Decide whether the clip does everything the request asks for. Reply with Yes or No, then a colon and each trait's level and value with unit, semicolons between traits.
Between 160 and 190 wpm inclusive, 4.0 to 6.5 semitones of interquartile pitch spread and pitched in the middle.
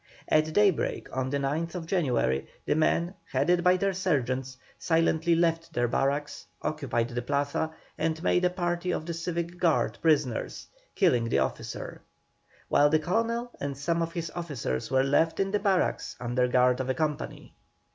Yes: average, 165 wpm; average, 4.7 semitones; medium, 160 Hz